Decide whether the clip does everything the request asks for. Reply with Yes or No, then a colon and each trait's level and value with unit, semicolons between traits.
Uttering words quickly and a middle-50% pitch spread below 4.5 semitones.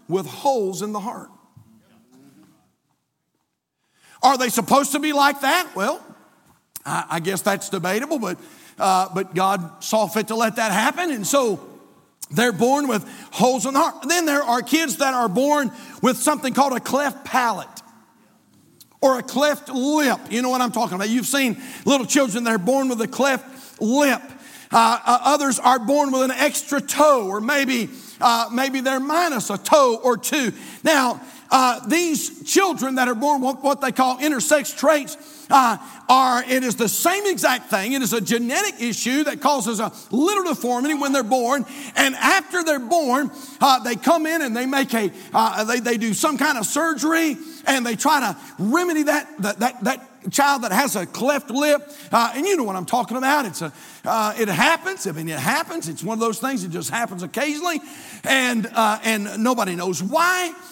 No: average, 185 wpm; average, 4.1 semitones